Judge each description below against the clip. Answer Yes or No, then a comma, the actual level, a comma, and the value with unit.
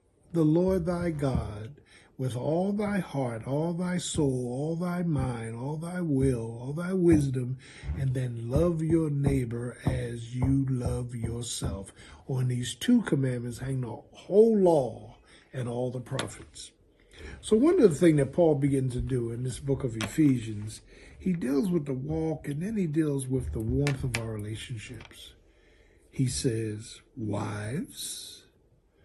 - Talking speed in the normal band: Yes, average, 155 wpm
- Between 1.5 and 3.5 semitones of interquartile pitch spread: No, average, 5.2 semitones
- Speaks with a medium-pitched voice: No, low, 130 Hz